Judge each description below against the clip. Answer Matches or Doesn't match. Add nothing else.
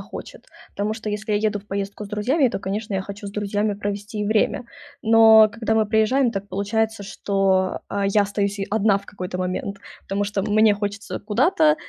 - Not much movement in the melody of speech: Matches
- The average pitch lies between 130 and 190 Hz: Doesn't match